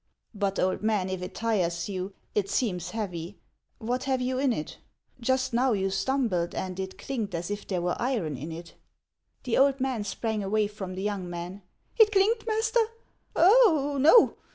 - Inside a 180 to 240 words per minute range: Yes, average, 185 wpm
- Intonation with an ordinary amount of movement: No, wide, 6.0 semitones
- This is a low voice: No, high, 210 Hz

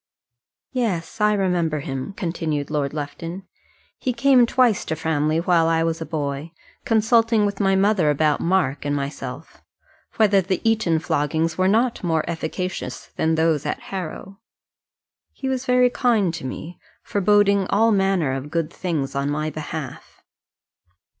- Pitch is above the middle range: No, medium, 170 Hz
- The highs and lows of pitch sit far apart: No, average, 4.9 semitones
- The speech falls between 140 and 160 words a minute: Yes, average, 145 wpm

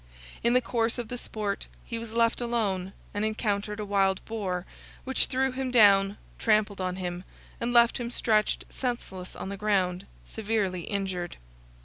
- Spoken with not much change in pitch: No, average, 3.3 semitones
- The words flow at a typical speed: Yes, average, 160 wpm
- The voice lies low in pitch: No, high, 210 Hz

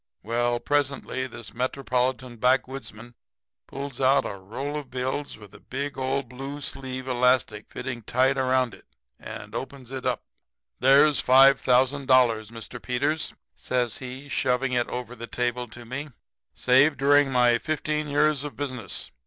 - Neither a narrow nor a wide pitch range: No, narrow, 2.0 semitones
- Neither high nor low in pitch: No, low, 130 Hz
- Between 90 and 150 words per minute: Yes, average, 140 wpm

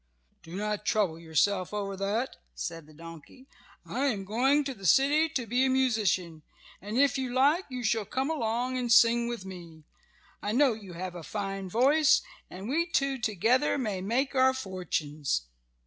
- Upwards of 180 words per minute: No, average, 175 wpm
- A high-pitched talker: Yes, high, 220 Hz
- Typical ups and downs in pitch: No, wide, 5.8 semitones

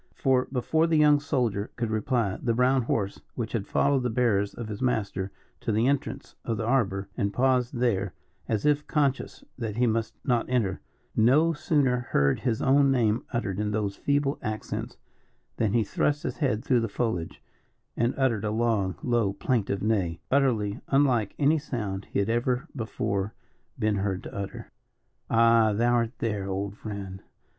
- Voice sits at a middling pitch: No, low, 115 Hz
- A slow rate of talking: No, average, 170 wpm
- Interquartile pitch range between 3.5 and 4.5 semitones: Yes, average, 4.0 semitones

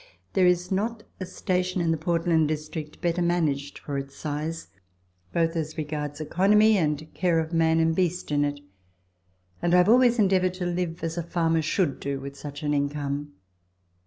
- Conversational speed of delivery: Yes, average, 180 wpm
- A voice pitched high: No, medium, 165 Hz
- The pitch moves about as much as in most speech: Yes, average, 3.2 semitones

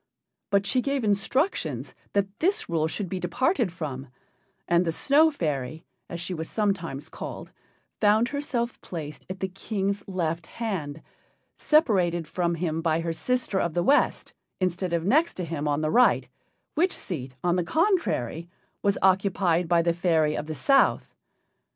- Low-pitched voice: No, medium, 180 Hz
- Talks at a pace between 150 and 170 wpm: Yes, average, 160 wpm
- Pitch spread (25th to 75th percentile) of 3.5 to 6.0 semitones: Yes, average, 4.8 semitones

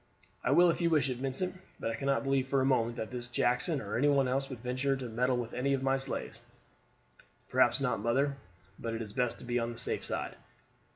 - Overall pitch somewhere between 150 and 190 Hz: No, low, 130 Hz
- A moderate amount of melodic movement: No, narrow, 2.2 semitones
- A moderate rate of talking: No, fast, 235 wpm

